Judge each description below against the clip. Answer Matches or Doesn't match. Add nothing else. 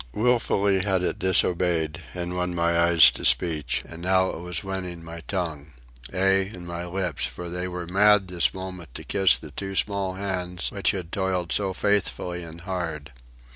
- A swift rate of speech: Doesn't match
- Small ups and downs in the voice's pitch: Matches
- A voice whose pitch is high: Doesn't match